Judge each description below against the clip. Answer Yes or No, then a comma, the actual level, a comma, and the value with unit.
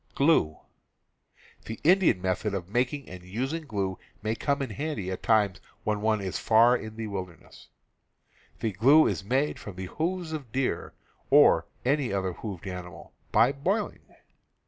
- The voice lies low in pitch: Yes, low, 110 Hz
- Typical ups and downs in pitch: No, wide, 6.6 semitones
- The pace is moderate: Yes, average, 155 wpm